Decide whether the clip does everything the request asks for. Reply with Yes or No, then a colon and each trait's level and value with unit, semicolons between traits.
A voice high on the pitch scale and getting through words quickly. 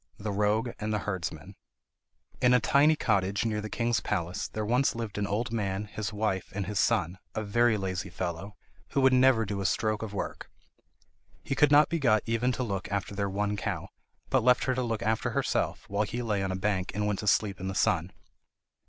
No: low, 105 Hz; fast, 220 wpm